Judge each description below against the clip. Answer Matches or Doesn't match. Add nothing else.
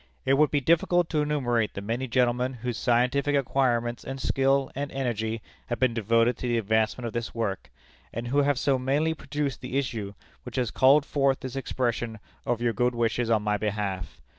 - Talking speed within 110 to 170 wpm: Doesn't match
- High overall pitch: Doesn't match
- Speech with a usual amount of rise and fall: Matches